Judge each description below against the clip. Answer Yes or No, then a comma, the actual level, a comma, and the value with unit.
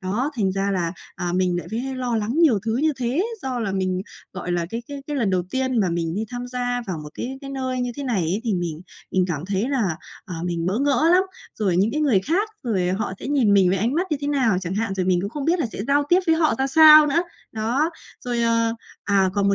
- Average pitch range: No, wide, 6.4 semitones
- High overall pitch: Yes, high, 225 Hz